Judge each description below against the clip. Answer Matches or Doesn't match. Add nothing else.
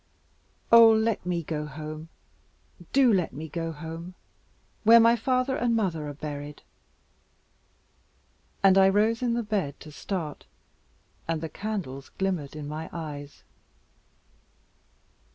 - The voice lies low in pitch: Doesn't match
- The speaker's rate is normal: Doesn't match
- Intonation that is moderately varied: Doesn't match